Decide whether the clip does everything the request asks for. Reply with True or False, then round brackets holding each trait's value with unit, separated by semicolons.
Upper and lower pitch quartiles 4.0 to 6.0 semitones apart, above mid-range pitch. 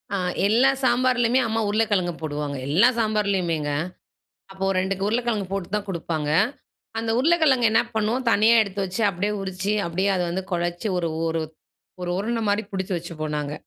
True (4.5 semitones; 195 Hz)